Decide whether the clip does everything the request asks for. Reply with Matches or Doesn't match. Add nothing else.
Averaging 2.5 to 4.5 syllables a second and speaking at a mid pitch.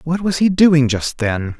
Matches